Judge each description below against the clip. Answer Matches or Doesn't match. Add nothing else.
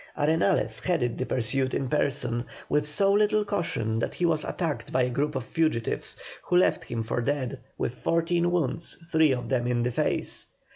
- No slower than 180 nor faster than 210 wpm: Matches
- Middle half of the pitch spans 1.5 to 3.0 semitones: Doesn't match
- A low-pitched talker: Doesn't match